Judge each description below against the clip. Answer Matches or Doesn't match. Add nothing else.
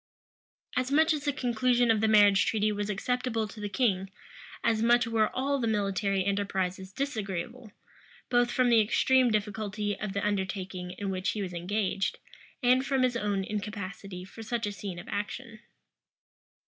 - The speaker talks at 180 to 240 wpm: Doesn't match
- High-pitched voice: Matches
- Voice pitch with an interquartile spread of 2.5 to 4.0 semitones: Matches